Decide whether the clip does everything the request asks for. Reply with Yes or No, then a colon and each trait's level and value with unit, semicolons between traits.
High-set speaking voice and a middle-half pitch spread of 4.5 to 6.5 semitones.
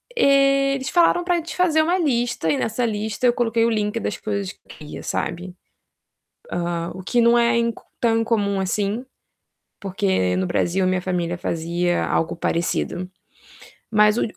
Yes: high, 210 Hz; average, 5.0 semitones